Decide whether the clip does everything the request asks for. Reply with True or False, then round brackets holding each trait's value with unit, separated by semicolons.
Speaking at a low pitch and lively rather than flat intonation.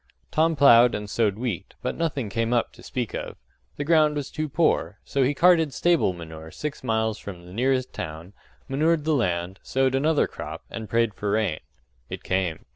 True (120 Hz; 6.5 semitones)